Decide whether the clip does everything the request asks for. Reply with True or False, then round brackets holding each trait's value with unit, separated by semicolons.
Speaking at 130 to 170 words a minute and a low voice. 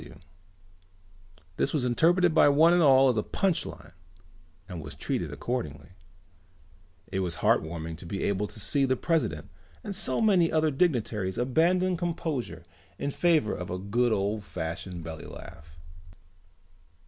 True (150 wpm; 125 Hz)